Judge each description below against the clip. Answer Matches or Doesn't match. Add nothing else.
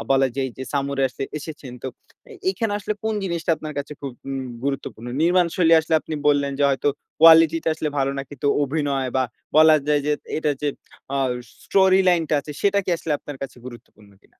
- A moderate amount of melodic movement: Matches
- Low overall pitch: Doesn't match